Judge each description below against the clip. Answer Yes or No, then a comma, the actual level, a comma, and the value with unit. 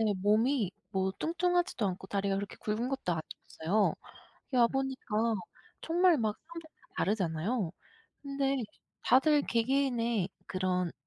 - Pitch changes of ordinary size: No, wide, 5.7 semitones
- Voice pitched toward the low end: No, high, 230 Hz